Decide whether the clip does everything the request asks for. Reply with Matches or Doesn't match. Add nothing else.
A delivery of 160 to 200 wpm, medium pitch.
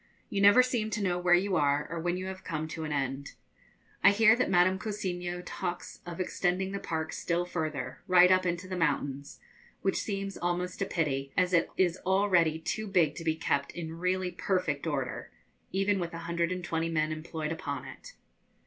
Matches